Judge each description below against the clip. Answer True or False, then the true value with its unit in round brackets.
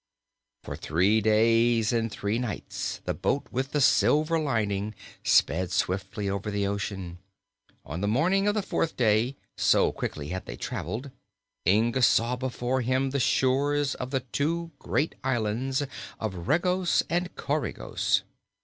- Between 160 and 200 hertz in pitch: False (120 Hz)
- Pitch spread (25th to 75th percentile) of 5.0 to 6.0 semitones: True (5.4 semitones)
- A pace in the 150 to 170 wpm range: False (140 wpm)